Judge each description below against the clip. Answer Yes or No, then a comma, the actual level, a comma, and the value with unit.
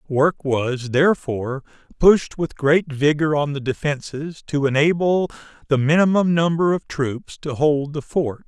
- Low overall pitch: No, medium, 150 Hz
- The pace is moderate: Yes, average, 150 wpm